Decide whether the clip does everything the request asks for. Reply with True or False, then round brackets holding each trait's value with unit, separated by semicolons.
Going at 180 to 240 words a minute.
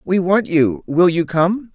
True (205 wpm)